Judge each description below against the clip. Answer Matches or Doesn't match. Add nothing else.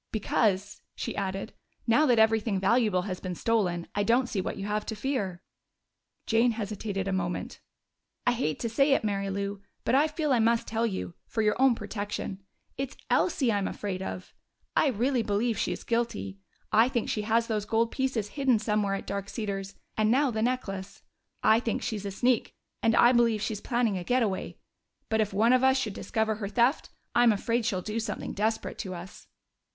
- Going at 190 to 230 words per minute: Matches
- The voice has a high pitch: Matches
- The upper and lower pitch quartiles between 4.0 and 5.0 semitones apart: Doesn't match